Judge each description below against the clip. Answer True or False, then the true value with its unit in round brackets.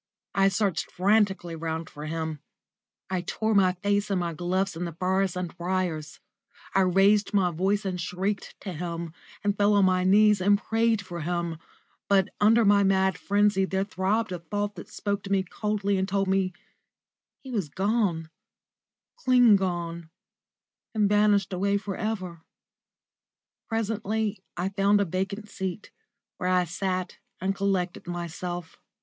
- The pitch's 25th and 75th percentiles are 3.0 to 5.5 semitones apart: False (2.5 semitones)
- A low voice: False (190 Hz)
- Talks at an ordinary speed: True (155 wpm)